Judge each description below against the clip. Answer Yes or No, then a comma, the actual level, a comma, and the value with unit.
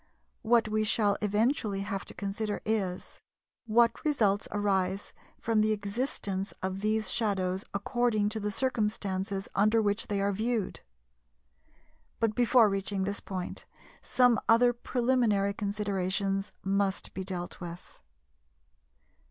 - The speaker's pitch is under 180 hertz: No, high, 205 Hz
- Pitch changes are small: Yes, narrow, 2.2 semitones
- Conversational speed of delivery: No, slow, 120 wpm